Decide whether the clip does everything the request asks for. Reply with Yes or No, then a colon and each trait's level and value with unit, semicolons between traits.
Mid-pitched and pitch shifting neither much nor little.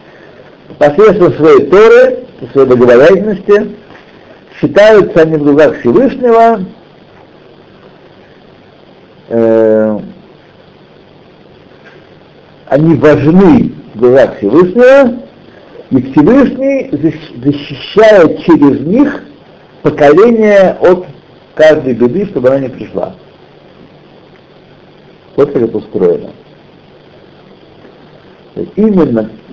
No: medium, 175 Hz; wide, 8.0 semitones